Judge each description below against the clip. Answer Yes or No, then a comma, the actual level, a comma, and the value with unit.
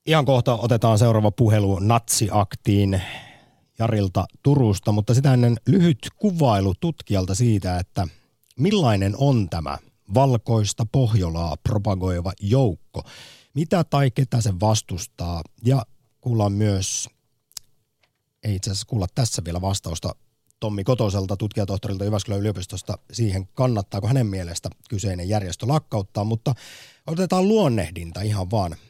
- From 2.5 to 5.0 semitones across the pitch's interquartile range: Yes, average, 4.5 semitones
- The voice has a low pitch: Yes, low, 110 Hz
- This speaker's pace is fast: No, average, 115 wpm